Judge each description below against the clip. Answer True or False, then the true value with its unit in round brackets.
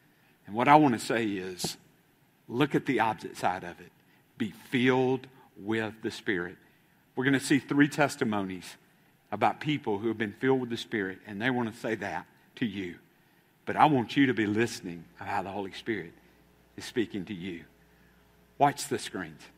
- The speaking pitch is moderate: False (110 Hz)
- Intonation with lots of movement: True (5.8 semitones)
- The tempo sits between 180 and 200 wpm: True (185 wpm)